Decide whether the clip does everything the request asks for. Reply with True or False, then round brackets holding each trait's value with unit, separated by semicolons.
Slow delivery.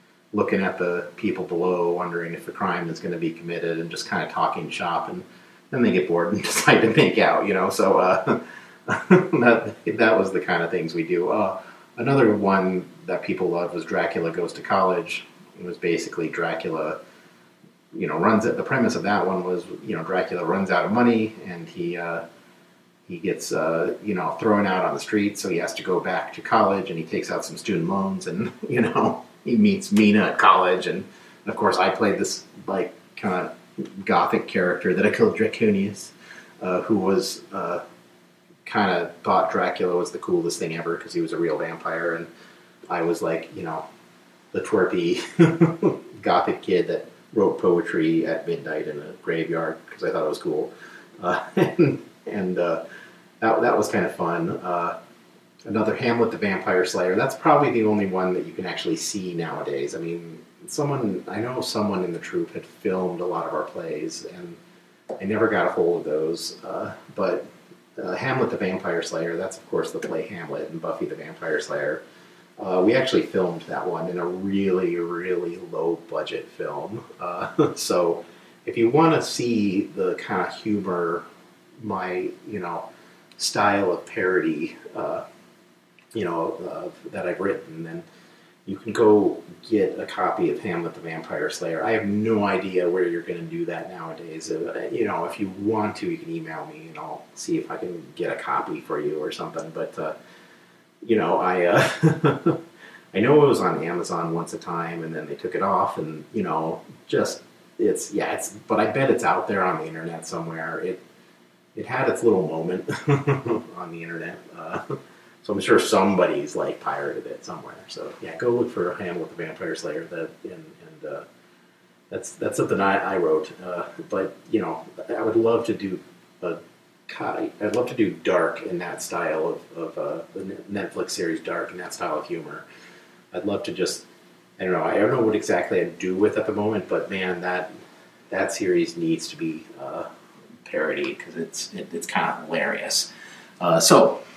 False (190 wpm)